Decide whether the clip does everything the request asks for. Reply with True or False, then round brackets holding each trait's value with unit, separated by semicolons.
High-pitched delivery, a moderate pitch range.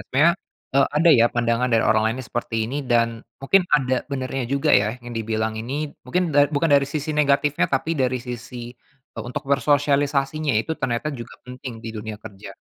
False (130 Hz; 3.5 semitones)